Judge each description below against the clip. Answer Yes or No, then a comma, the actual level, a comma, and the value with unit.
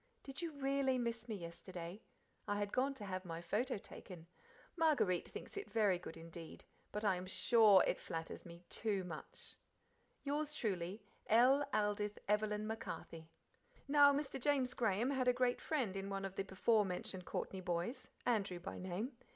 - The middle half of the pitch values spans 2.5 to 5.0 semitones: No, wide, 5.5 semitones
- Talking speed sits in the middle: Yes, average, 165 wpm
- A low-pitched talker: No, high, 210 Hz